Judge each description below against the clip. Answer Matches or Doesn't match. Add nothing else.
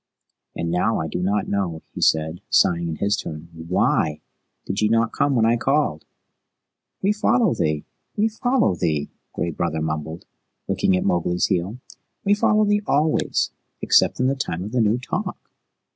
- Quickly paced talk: Doesn't match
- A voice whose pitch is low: Matches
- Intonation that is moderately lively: Doesn't match